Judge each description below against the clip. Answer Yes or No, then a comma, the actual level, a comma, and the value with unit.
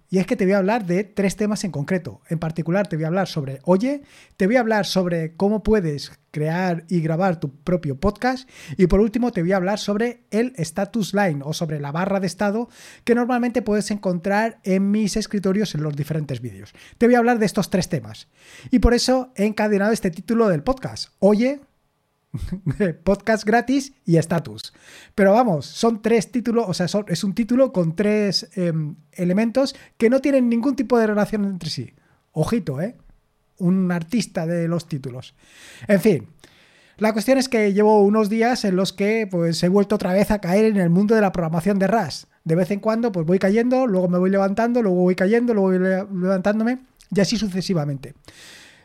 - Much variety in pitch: No, average, 4.3 semitones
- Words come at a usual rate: No, fast, 200 wpm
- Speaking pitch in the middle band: No, high, 195 Hz